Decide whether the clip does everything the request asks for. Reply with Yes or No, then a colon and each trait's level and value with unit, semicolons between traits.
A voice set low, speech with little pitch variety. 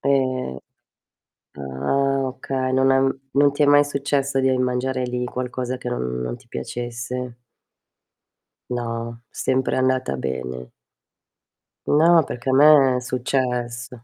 Yes: low, 125 Hz; narrow, 2.0 semitones